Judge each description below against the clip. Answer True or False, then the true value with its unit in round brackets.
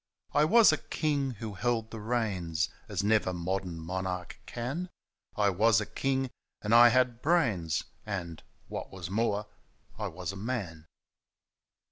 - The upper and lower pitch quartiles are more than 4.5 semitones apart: True (4.9 semitones)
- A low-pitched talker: True (105 Hz)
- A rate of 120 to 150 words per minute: True (145 wpm)